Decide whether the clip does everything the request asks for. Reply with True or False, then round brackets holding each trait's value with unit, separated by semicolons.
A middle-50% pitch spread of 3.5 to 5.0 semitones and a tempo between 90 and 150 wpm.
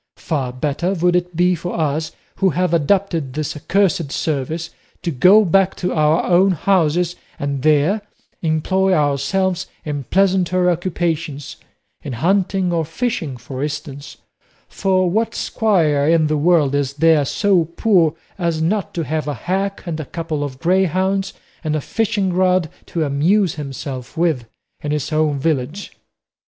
True (4.0 semitones; 145 wpm)